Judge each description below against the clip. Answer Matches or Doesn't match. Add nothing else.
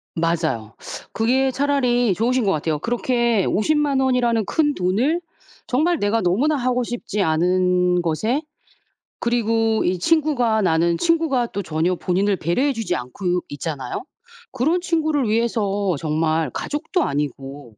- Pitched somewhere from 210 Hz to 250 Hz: Matches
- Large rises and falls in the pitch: Matches